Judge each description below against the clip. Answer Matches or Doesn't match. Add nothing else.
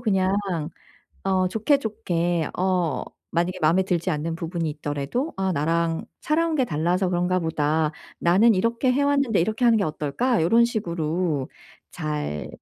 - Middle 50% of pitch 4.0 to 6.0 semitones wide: Matches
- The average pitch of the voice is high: Doesn't match